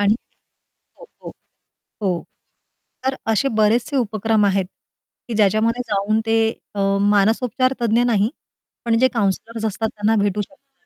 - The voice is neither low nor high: No, high, 220 Hz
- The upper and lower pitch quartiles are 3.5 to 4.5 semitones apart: No, narrow, 2.4 semitones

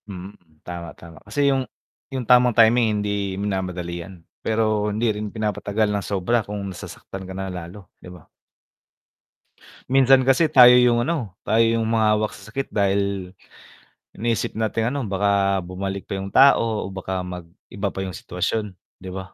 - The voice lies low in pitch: Yes, low, 105 Hz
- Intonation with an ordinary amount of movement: Yes, average, 3.2 semitones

